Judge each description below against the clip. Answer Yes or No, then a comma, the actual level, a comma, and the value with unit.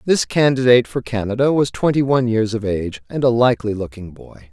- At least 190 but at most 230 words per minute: Yes, average, 200 wpm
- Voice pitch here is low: Yes, low, 120 Hz